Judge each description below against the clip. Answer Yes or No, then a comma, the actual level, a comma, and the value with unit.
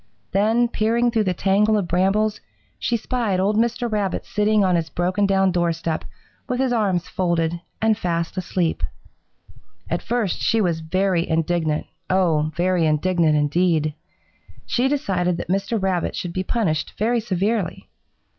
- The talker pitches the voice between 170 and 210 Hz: Yes, medium, 185 Hz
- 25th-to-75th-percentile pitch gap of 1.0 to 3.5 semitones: No, average, 4.0 semitones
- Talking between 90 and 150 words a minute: Yes, average, 145 wpm